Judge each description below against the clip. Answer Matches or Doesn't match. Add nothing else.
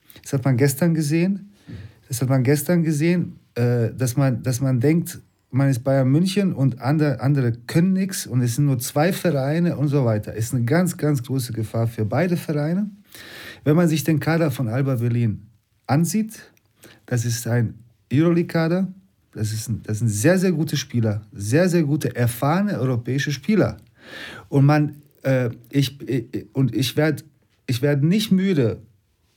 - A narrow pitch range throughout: Doesn't match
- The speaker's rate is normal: Matches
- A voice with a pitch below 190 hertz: Matches